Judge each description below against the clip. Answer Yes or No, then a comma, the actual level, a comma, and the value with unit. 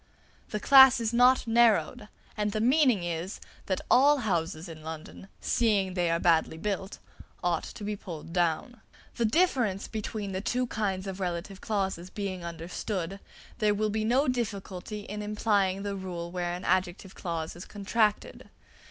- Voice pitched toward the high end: Yes, high, 195 Hz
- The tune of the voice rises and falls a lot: No, average, 3.7 semitones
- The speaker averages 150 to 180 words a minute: Yes, average, 160 wpm